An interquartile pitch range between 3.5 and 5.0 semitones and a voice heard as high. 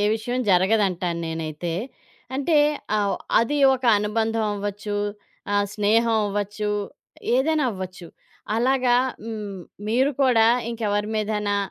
No: narrow, 2.6 semitones; high, 210 Hz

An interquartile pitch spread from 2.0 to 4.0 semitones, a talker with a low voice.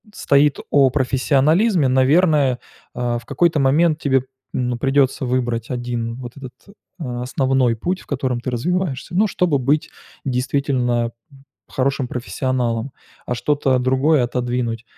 Yes: average, 2.7 semitones; low, 130 Hz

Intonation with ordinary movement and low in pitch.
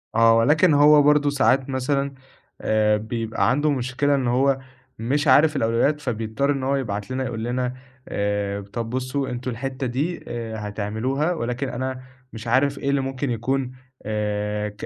Yes: average, 3.6 semitones; low, 130 Hz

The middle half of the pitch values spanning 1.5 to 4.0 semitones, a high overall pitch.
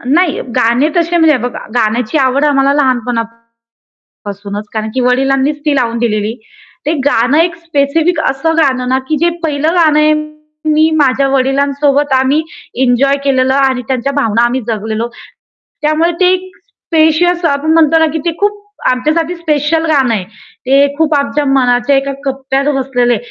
Yes: average, 3.6 semitones; very high, 280 Hz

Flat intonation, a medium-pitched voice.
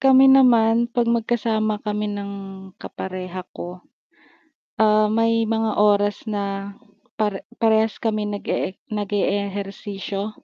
No: narrow, 2.0 semitones; high, 210 Hz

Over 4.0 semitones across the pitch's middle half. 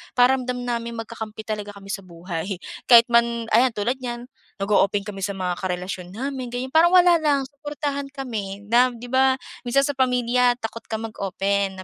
Yes: average, 4.4 semitones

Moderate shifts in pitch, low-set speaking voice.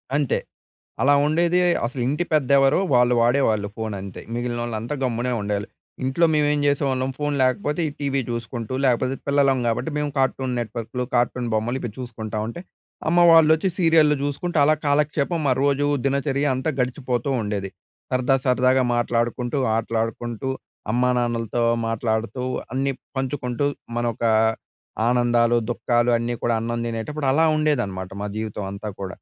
Yes: average, 3.3 semitones; low, 125 Hz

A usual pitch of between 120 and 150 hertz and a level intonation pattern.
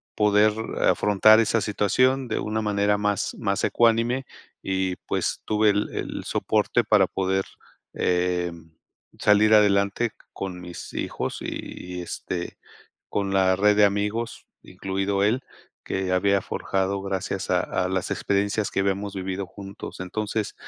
No: low, 100 Hz; narrow, 1.8 semitones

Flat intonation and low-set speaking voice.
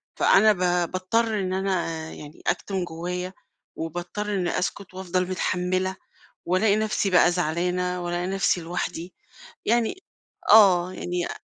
No: narrow, 1.7 semitones; medium, 185 Hz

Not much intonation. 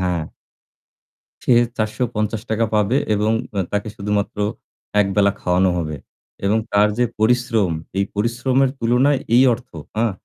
No: average, 3.1 semitones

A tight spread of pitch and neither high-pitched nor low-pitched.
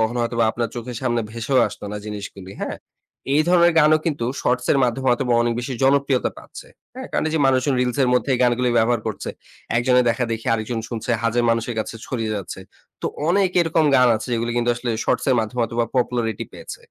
No: narrow, 2.2 semitones; low, 120 Hz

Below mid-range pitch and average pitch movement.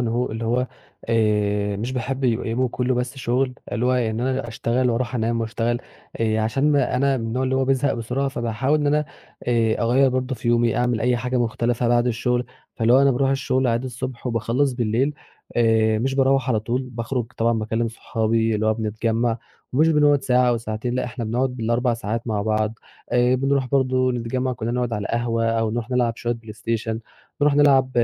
No: low, 120 Hz; narrow, 2.2 semitones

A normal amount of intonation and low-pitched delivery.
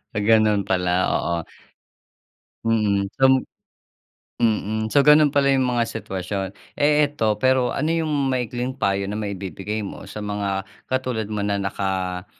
Yes: average, 4.7 semitones; low, 110 Hz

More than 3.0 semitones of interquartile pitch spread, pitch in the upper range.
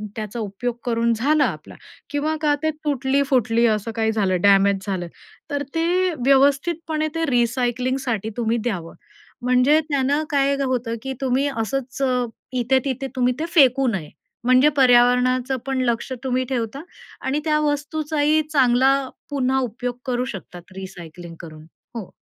Yes: average, 3.5 semitones; very high, 255 Hz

